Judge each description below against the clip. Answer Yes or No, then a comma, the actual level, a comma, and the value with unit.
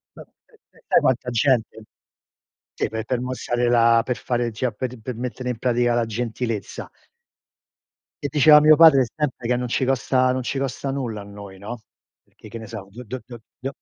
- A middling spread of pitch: No, narrow, 2.1 semitones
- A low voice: Yes, low, 125 Hz